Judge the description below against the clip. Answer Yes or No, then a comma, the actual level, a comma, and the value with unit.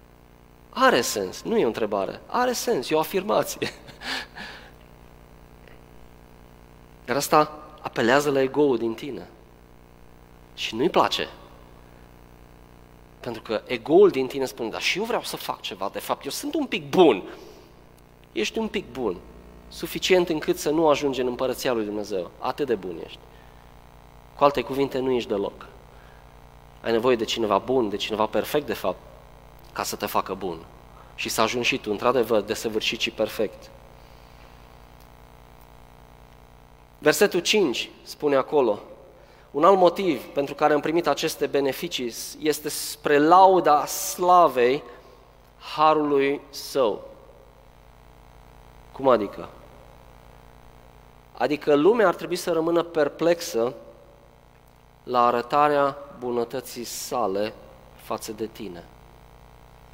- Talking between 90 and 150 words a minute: Yes, average, 125 wpm